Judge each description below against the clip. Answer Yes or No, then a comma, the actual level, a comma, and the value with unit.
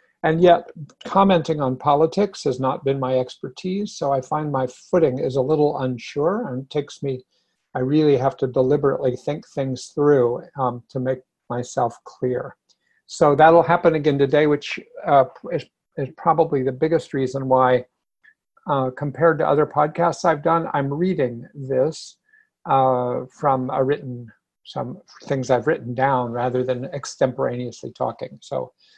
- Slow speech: No, average, 150 wpm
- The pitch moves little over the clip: No, average, 3.8 semitones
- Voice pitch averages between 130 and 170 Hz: Yes, medium, 140 Hz